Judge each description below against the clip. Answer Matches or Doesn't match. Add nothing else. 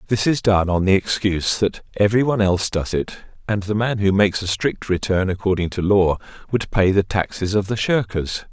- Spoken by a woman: Doesn't match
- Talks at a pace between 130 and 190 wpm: Doesn't match